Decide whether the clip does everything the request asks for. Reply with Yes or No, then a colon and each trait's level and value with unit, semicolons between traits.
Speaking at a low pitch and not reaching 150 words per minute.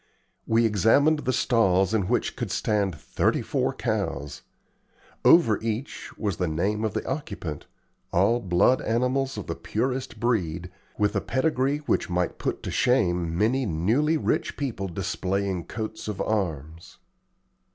Yes: low, 105 Hz; average, 140 wpm